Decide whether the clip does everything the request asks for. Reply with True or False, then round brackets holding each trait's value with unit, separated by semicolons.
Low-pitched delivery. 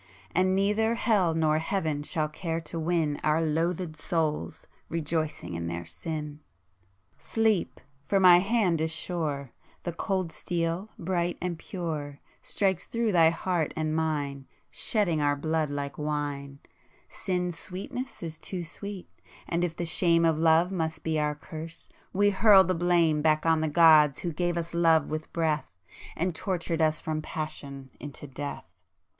False (160 Hz)